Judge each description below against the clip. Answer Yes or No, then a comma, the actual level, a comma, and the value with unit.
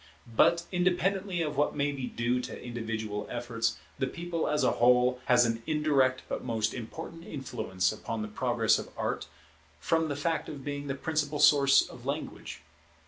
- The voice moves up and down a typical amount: Yes, average, 4.6 semitones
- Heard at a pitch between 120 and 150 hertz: Yes, low, 135 Hz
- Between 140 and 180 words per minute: Yes, average, 170 wpm